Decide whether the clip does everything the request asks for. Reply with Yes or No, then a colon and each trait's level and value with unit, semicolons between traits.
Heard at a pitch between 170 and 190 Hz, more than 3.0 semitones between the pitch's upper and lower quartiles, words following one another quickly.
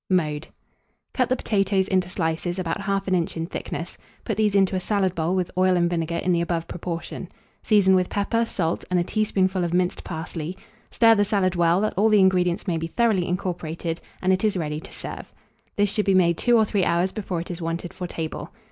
No: medium, 185 Hz; average, 2.7 semitones; fast, 215 wpm